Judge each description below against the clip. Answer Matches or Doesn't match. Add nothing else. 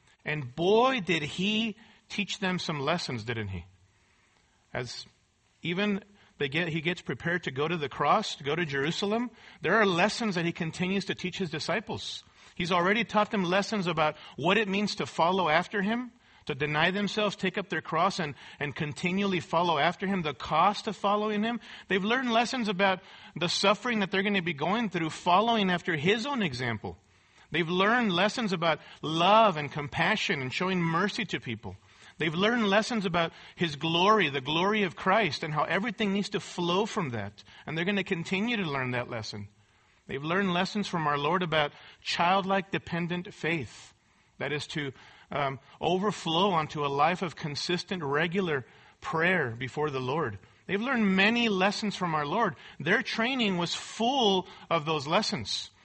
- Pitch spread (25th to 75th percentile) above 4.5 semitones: Matches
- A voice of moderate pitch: Matches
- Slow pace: Doesn't match